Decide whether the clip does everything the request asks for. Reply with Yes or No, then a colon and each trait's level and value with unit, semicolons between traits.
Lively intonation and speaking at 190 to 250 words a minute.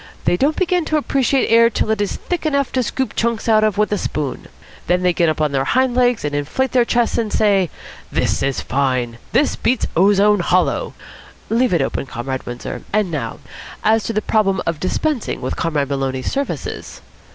Yes: wide, 8.4 semitones; average, 195 wpm